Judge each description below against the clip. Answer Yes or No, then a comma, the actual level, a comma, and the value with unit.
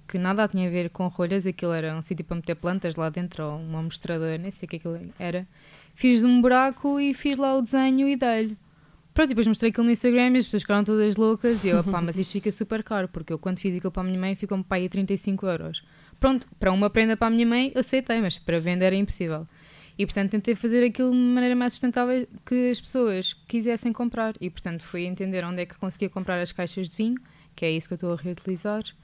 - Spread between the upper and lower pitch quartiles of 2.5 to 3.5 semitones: No, average, 4.9 semitones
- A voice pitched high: Yes, high, 195 Hz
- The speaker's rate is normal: No, fast, 245 wpm